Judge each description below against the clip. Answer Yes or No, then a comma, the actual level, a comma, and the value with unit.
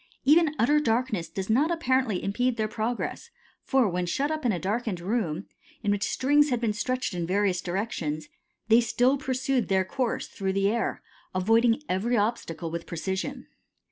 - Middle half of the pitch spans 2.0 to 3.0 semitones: No, average, 5.1 semitones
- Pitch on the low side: No, high, 225 Hz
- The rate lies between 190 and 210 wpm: No, average, 170 wpm